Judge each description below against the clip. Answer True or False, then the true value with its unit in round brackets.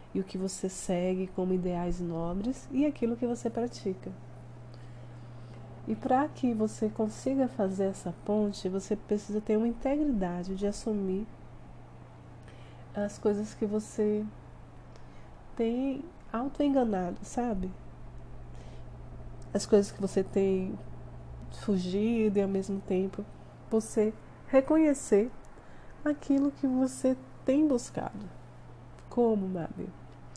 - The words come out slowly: True (105 wpm)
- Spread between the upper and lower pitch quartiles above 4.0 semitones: True (4.5 semitones)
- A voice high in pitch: True (205 Hz)